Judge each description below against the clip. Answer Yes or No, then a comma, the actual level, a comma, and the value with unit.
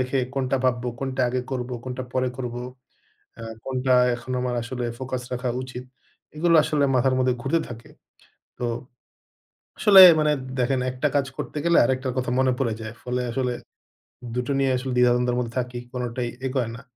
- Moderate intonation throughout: No, narrow, 1.3 semitones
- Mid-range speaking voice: No, low, 130 Hz